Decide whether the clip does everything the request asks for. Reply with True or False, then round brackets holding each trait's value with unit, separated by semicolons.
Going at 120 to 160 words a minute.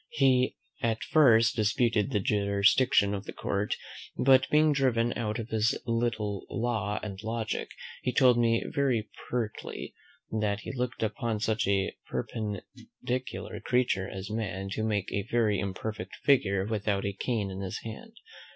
True (150 wpm)